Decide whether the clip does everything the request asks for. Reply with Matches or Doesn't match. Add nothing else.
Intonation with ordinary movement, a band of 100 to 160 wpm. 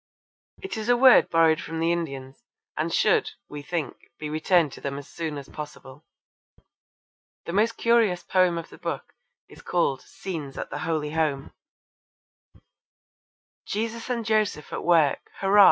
Doesn't match